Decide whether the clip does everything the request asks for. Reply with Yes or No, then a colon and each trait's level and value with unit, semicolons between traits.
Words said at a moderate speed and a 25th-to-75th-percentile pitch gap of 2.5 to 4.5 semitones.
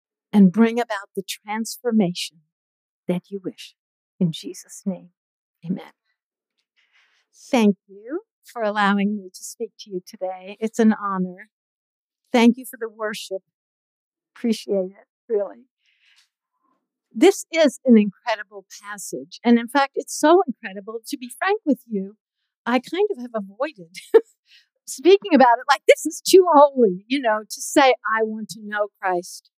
No: average, 145 wpm; average, 5.2 semitones